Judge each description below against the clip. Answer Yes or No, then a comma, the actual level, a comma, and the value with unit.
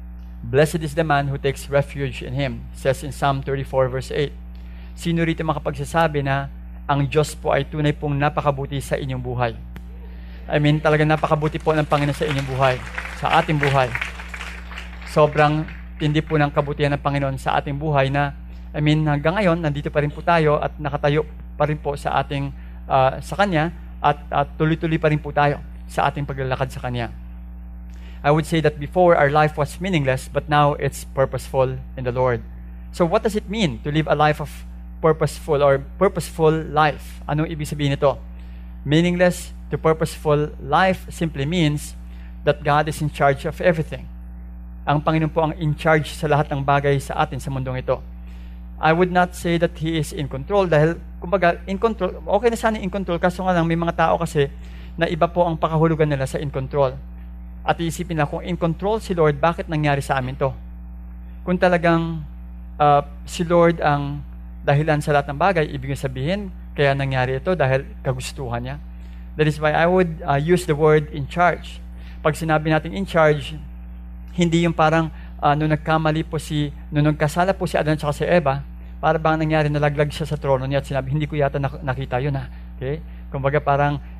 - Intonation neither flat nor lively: Yes, average, 3.5 semitones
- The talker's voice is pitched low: No, medium, 145 Hz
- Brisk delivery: No, average, 185 wpm